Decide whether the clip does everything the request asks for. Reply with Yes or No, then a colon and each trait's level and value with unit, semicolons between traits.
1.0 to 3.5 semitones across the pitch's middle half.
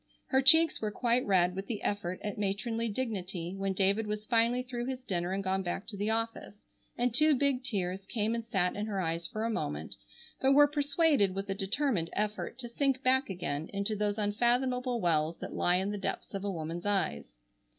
No: average, 4.4 semitones